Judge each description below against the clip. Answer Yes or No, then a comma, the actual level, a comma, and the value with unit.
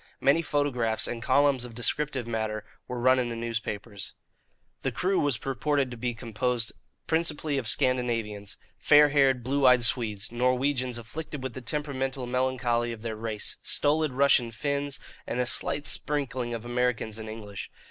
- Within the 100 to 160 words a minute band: Yes, average, 155 wpm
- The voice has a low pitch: Yes, low, 125 Hz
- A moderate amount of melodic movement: Yes, average, 3.4 semitones